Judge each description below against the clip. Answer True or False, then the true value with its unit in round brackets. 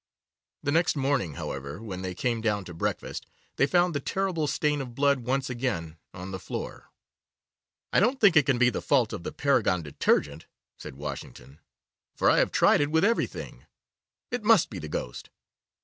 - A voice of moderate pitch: False (125 Hz)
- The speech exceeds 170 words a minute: True (180 wpm)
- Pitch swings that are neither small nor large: False (8.4 semitones)